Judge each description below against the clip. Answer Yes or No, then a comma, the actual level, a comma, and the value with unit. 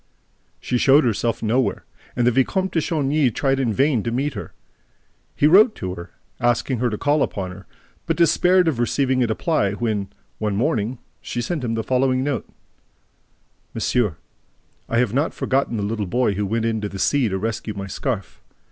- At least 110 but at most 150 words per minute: No, average, 180 wpm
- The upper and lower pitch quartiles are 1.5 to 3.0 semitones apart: No, average, 4.4 semitones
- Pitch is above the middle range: No, low, 120 Hz